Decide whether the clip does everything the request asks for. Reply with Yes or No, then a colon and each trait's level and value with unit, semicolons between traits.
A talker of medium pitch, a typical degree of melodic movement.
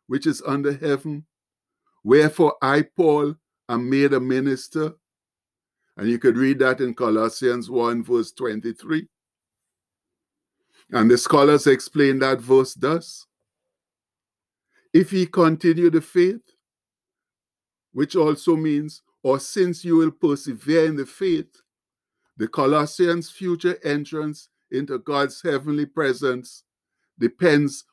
Yes: medium, 145 Hz; average, 3.6 semitones